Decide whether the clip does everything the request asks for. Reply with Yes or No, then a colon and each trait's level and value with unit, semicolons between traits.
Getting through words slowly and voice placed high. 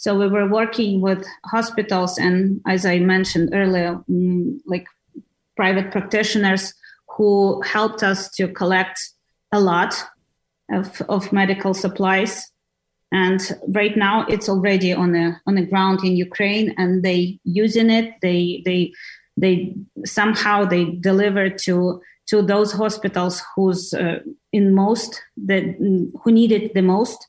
Yes: slow, 130 wpm; high, 195 Hz